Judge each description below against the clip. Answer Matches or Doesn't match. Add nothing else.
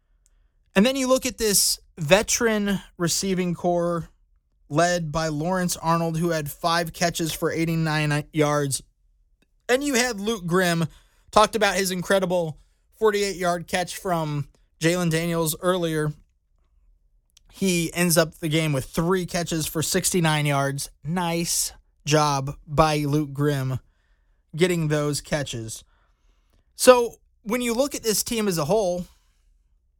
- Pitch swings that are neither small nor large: Matches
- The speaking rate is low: Matches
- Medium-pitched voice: Matches